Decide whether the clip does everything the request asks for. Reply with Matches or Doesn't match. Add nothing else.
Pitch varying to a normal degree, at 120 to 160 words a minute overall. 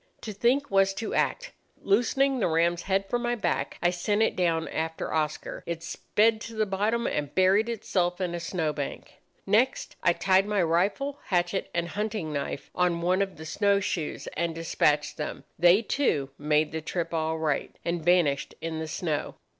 Doesn't match